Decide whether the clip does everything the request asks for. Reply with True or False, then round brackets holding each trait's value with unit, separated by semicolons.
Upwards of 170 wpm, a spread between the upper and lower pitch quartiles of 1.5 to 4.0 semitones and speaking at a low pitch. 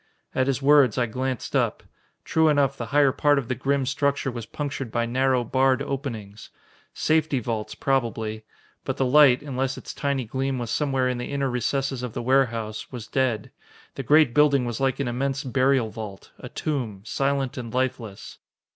True (180 wpm; 2.6 semitones; 130 Hz)